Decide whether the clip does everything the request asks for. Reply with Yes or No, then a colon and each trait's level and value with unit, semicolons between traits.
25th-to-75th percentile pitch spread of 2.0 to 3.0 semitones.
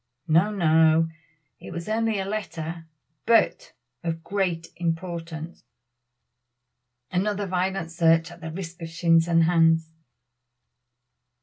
Yes: narrow, 2.6 semitones